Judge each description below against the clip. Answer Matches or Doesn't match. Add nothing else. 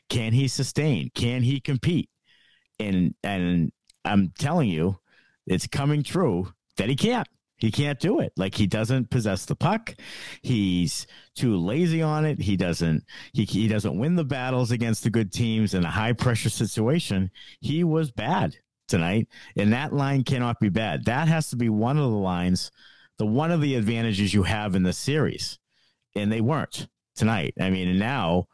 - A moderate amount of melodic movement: Doesn't match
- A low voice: Matches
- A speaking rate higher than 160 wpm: Matches